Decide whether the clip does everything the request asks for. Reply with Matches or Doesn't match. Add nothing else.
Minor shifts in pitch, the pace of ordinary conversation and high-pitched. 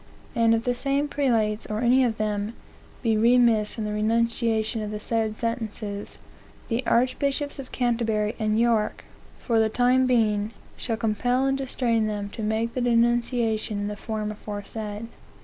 Matches